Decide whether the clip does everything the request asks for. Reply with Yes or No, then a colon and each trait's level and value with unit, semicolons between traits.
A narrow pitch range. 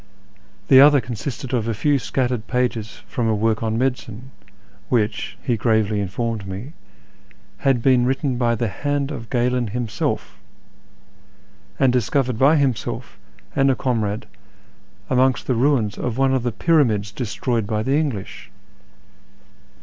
No: average, 3.3 semitones